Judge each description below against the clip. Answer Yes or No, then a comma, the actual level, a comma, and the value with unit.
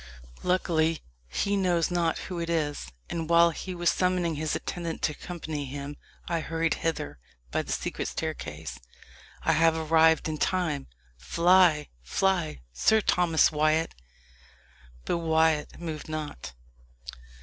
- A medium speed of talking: No, slow, 130 wpm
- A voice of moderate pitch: Yes, medium, 160 Hz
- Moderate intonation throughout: No, narrow, 2.0 semitones